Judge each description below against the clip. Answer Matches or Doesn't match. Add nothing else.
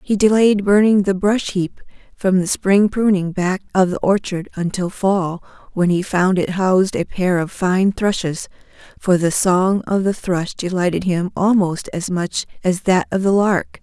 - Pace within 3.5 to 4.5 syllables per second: Matches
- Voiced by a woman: Matches